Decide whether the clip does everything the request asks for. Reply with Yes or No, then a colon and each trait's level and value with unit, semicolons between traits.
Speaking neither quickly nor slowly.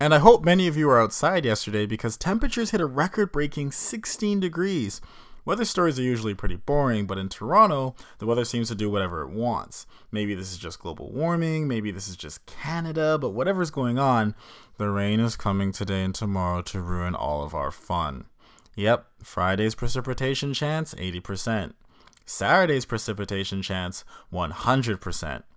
Yes: average, 165 wpm